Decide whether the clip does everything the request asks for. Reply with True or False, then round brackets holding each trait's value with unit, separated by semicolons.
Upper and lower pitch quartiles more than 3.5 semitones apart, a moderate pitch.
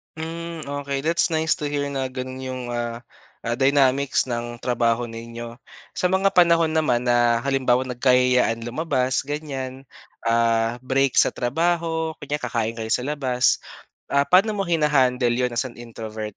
False (3.9 semitones; 130 Hz)